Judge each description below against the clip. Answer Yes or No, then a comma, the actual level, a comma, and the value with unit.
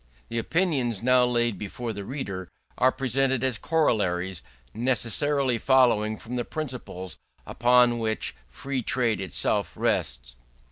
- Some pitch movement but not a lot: Yes, average, 3.7 semitones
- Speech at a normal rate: No, slow, 125 wpm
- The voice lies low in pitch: Yes, low, 120 Hz